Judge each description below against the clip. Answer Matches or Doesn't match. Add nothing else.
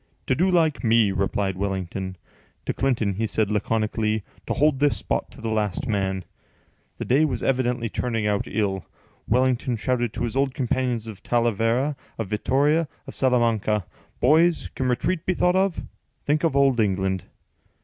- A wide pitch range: Doesn't match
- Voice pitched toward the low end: Matches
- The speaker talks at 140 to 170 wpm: Matches